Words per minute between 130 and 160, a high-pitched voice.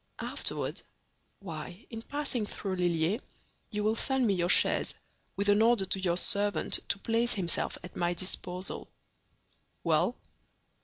Yes: average, 140 wpm; high, 200 Hz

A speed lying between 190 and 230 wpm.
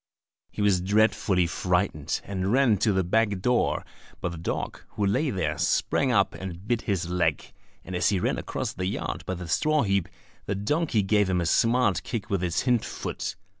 Yes: average, 195 wpm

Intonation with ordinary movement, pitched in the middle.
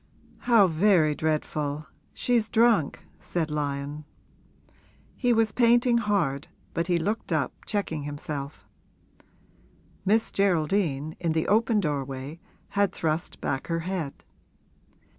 No: wide, 5.8 semitones; medium, 165 Hz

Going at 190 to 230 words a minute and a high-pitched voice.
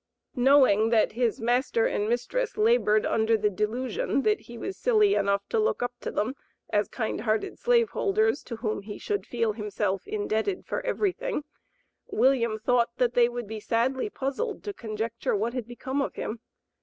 No: average, 175 wpm; high, 240 Hz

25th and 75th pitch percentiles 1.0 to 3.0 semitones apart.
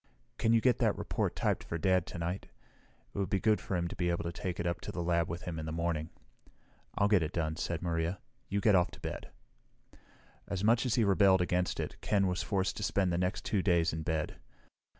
Yes: average, 2.7 semitones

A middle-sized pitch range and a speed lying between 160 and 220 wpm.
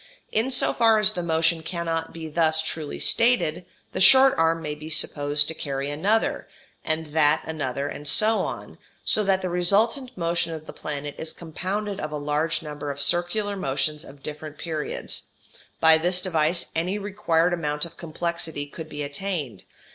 Yes: average, 3.4 semitones; average, 170 wpm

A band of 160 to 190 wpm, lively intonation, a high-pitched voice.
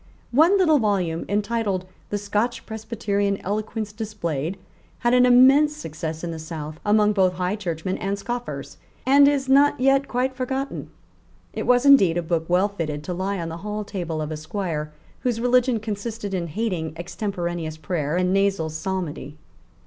Yes: average, 165 wpm; wide, 6.0 semitones; high, 200 Hz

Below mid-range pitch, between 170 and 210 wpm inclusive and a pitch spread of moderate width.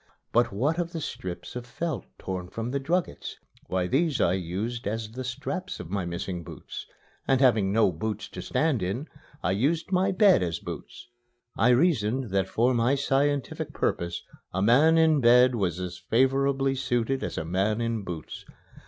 No: low, 120 Hz; average, 175 wpm; wide, 6.2 semitones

